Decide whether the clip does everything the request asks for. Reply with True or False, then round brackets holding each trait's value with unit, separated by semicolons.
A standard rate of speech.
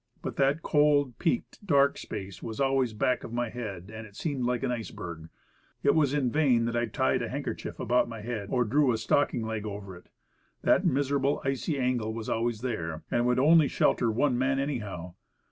False (210 wpm)